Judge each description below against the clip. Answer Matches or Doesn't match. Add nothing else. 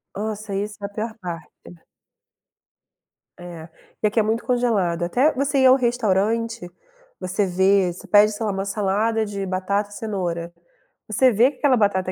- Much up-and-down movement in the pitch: Doesn't match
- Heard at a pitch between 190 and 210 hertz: Matches